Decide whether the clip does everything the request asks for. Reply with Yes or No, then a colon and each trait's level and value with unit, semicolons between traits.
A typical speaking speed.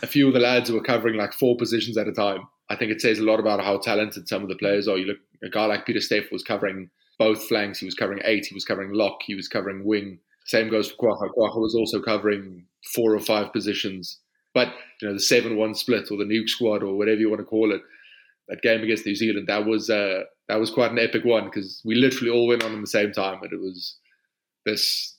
No: fast, 255 wpm